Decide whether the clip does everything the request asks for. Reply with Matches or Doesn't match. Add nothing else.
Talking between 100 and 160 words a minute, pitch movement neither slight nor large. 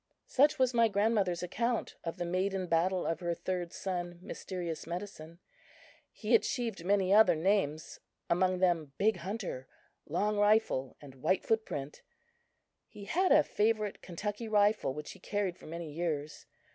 Matches